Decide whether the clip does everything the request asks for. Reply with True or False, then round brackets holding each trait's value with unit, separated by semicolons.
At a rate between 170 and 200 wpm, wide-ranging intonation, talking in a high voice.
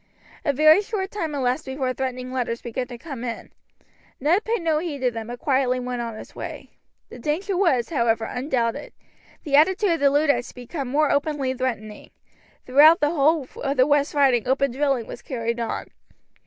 False (185 wpm; 3.7 semitones; 270 Hz)